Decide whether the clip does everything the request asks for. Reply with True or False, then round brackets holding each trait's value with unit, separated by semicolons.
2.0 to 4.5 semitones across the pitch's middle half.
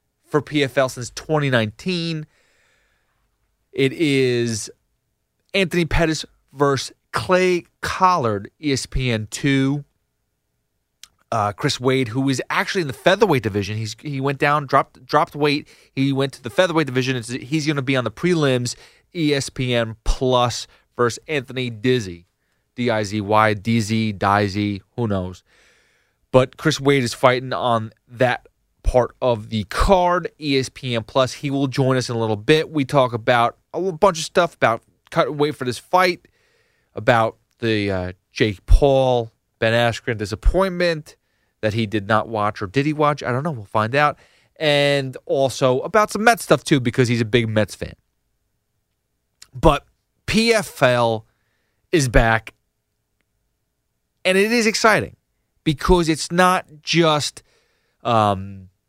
False (5.1 semitones)